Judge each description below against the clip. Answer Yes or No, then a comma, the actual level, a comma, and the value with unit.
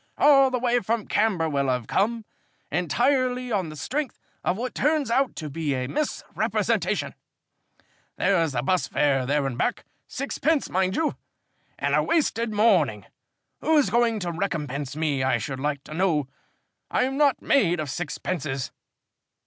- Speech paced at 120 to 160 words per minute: Yes, average, 150 wpm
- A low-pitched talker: No, medium, 185 Hz